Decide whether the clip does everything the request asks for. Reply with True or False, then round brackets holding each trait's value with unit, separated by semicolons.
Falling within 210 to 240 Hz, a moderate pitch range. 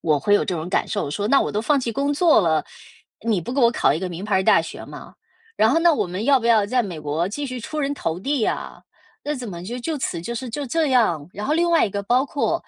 False (230 Hz; 7.1 semitones)